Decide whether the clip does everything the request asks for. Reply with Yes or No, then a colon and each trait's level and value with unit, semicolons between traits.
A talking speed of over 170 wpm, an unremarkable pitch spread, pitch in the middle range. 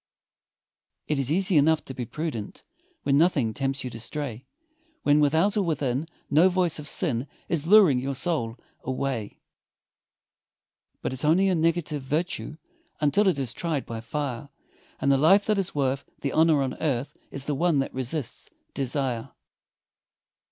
No: average, 160 wpm; average, 3.8 semitones; medium, 145 Hz